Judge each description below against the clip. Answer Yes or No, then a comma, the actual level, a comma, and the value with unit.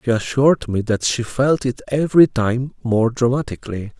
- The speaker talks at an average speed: Yes, average, 165 wpm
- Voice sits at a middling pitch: No, low, 125 Hz